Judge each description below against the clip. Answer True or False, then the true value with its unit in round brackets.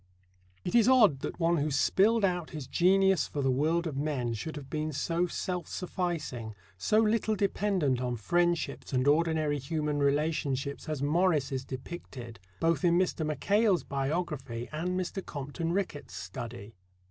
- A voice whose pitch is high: False (155 Hz)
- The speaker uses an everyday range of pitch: True (4.6 semitones)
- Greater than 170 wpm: False (155 wpm)